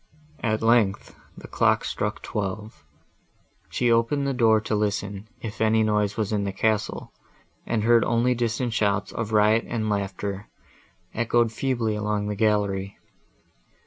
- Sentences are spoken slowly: No, average, 145 wpm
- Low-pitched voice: Yes, low, 110 Hz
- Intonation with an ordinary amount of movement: No, narrow, 2.0 semitones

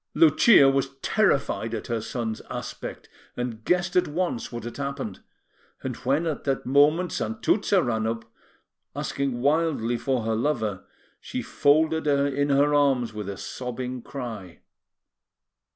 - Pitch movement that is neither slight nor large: Yes, average, 4.1 semitones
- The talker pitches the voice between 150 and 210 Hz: No, low, 135 Hz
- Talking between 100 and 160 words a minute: Yes, average, 140 wpm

